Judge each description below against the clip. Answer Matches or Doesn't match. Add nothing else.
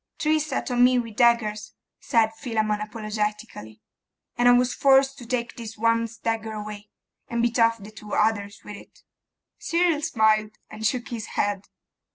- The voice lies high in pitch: Matches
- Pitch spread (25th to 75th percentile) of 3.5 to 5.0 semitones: Doesn't match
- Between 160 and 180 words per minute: Matches